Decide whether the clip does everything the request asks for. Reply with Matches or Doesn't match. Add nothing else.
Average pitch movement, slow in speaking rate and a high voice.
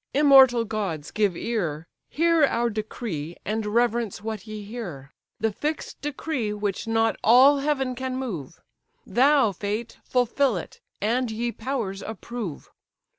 Matches